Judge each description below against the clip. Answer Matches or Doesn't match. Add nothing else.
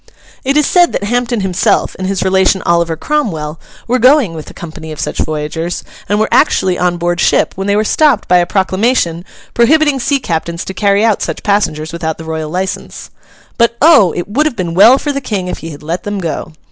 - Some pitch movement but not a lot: Doesn't match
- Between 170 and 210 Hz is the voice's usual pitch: Matches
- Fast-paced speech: Matches